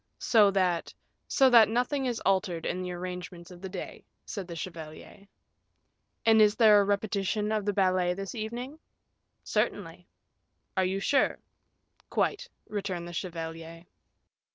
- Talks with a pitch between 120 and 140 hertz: No, high, 195 Hz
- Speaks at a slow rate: No, average, 145 wpm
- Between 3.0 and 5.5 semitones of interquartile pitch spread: Yes, average, 3.4 semitones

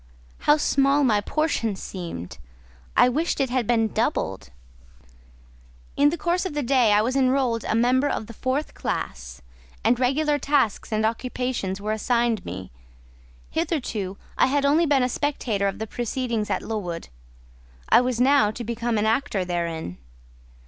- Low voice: No, high, 240 Hz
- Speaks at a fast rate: No, average, 155 wpm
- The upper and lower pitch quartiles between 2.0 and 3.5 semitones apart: No, average, 4.7 semitones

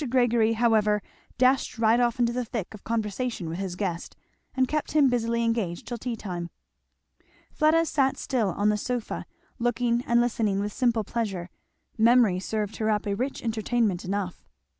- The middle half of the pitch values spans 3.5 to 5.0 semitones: No, average, 3.0 semitones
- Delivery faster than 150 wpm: Yes, average, 165 wpm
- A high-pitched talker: Yes, high, 225 Hz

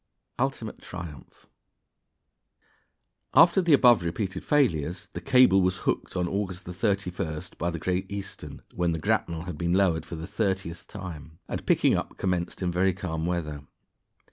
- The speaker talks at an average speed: Yes, average, 150 wpm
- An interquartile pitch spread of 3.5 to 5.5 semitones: No, average, 2.7 semitones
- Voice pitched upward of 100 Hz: No, very low, 90 Hz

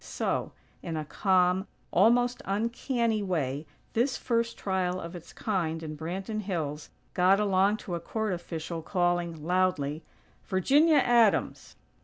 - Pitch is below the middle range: No, medium, 185 Hz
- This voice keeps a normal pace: No, slow, 130 wpm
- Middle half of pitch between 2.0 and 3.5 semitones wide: No, average, 4.6 semitones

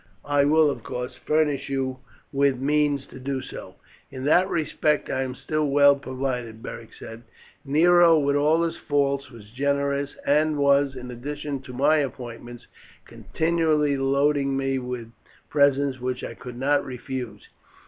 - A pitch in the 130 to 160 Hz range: Yes, medium, 140 Hz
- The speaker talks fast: No, average, 150 wpm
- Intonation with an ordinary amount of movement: No, narrow, 2.2 semitones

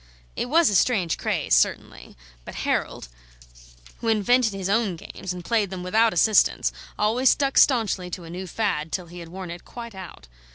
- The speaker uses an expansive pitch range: No, average, 4.3 semitones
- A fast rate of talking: No, average, 180 wpm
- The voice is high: Yes, high, 195 Hz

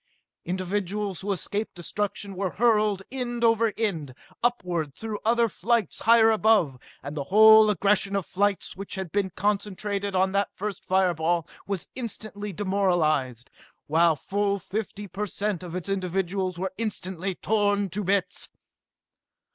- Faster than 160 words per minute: No, average, 140 wpm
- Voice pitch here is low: No, high, 200 Hz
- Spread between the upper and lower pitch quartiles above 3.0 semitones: No, narrow, 2.5 semitones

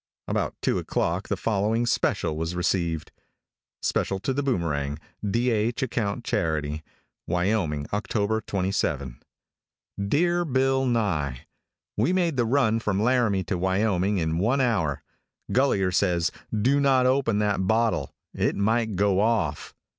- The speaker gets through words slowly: Yes, slow, 130 wpm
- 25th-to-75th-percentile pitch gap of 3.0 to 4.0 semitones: No, wide, 5.4 semitones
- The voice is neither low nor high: No, low, 105 Hz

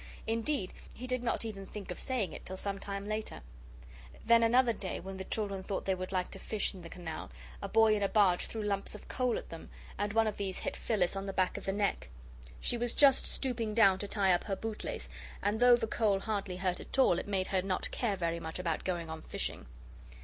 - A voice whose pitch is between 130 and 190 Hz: No, high, 200 Hz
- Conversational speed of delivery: No, fast, 235 wpm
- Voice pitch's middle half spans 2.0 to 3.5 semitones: Yes, average, 3.1 semitones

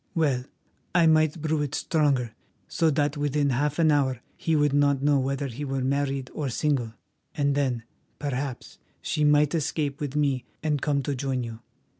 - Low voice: No, medium, 145 Hz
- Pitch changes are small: Yes, narrow, 1.9 semitones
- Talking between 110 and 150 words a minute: No, average, 175 wpm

